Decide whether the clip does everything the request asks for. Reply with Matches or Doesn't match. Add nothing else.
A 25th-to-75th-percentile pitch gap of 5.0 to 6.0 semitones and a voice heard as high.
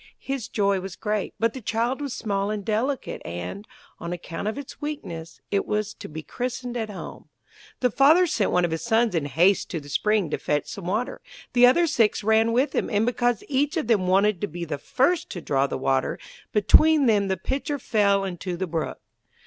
Matches